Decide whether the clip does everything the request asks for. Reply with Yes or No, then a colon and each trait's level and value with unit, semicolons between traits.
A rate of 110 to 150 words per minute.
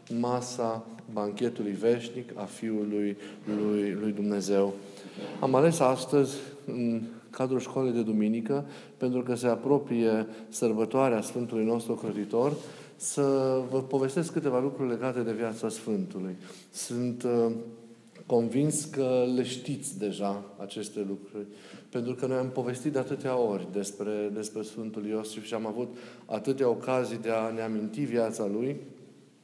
Yes: average, 130 wpm